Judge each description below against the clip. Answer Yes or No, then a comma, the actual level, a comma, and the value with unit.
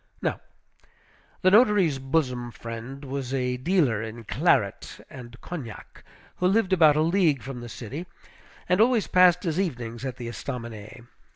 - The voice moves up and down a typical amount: No, wide, 6.9 semitones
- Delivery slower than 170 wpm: Yes, average, 150 wpm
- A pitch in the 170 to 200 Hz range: No, low, 135 Hz